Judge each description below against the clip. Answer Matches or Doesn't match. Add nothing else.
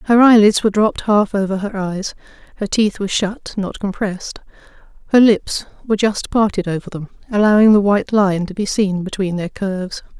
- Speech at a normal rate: Matches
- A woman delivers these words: Matches